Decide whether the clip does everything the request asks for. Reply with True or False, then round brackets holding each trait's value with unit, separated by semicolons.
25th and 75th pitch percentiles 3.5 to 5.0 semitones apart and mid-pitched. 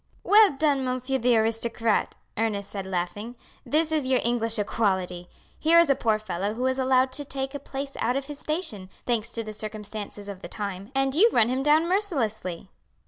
False (4.6 semitones; 240 Hz)